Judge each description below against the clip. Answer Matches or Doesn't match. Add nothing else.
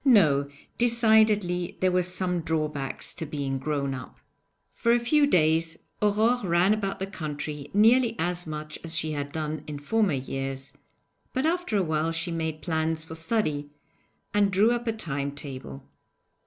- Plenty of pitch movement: Matches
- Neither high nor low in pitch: Matches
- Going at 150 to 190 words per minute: Matches